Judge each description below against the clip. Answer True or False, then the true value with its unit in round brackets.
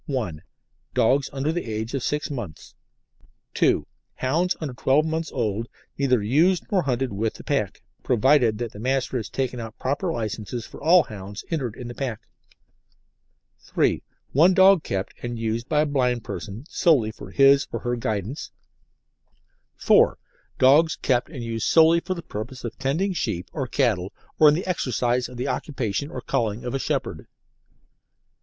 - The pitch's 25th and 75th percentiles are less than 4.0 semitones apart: False (4.7 semitones)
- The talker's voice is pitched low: True (130 Hz)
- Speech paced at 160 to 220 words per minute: True (165 wpm)